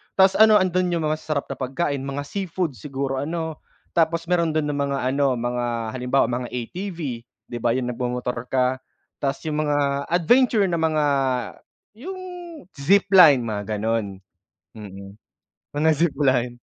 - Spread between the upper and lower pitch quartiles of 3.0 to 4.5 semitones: No, average, 5.2 semitones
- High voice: No, medium, 140 Hz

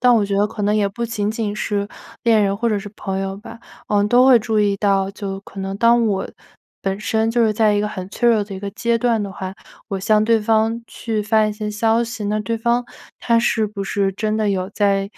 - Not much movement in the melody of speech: Yes, narrow, 2.1 semitones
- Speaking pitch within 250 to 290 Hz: No, high, 210 Hz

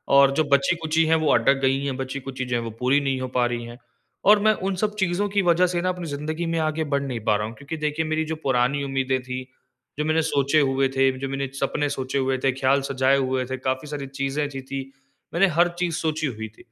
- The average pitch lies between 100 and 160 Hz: Yes, medium, 140 Hz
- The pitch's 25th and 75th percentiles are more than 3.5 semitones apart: No, average, 3.1 semitones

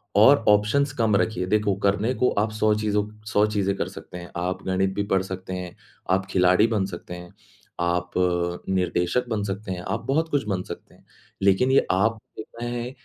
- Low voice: Yes, low, 100 Hz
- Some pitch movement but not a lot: Yes, average, 3.1 semitones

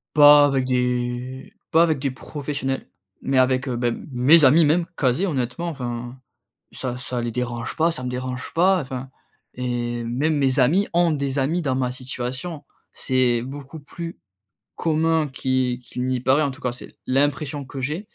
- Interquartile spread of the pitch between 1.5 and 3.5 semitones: Yes, average, 3.1 semitones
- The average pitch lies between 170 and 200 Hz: No, low, 130 Hz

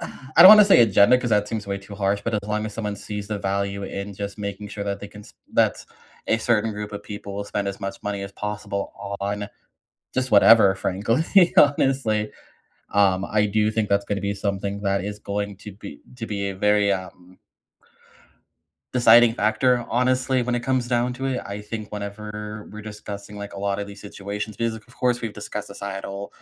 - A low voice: Yes, low, 105 Hz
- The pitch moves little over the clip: Yes, narrow, 1.9 semitones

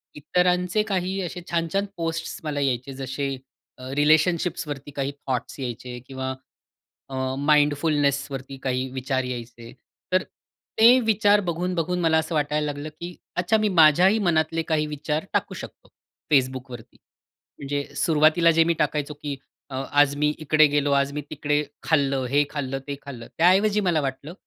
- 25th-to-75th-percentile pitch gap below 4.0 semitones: Yes, average, 3.6 semitones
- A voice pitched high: No, medium, 150 Hz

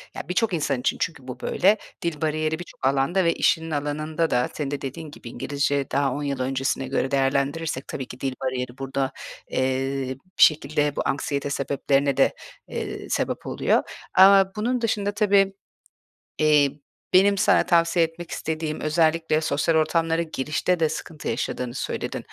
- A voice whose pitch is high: No, medium, 150 Hz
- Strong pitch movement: No, average, 3.5 semitones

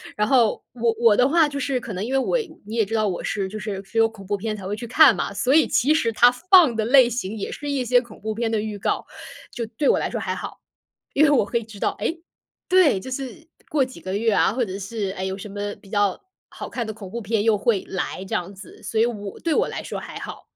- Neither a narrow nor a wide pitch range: Yes, average, 3.8 semitones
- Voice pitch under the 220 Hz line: No, high, 225 Hz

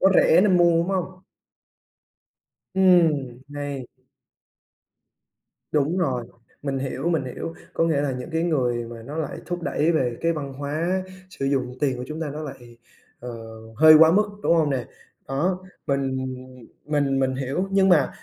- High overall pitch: No, medium, 145 Hz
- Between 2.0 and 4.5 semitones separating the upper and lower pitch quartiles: Yes, average, 4.2 semitones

